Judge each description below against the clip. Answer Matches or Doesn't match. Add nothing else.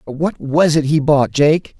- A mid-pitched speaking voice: Matches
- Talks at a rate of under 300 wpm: Matches